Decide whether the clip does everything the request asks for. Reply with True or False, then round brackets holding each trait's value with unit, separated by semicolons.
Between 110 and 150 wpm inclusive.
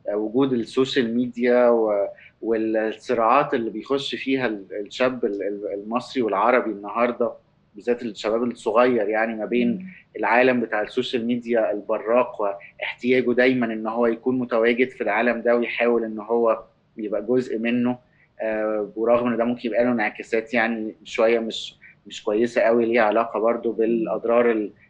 True (130 wpm)